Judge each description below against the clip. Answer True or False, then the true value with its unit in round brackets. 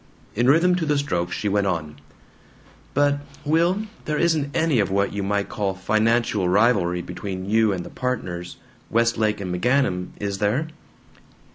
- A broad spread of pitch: True (6.8 semitones)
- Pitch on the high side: False (105 Hz)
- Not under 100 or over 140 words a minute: False (155 wpm)